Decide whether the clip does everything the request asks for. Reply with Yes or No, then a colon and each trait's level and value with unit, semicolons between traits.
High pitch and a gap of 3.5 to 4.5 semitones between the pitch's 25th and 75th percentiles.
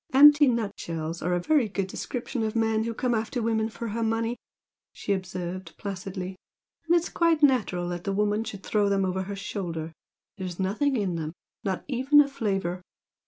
Yes: high, 205 Hz; average, 4.1 semitones